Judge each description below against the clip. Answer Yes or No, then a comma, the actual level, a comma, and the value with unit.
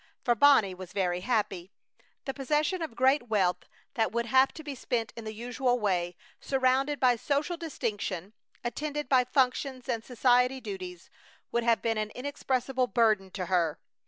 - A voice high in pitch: Yes, high, 240 Hz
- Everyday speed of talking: Yes, average, 160 wpm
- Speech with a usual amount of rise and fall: Yes, average, 4.3 semitones